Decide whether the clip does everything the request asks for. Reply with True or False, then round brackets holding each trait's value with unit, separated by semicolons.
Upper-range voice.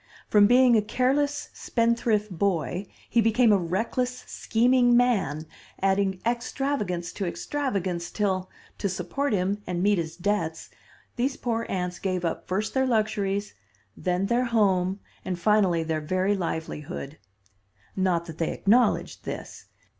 True (200 Hz)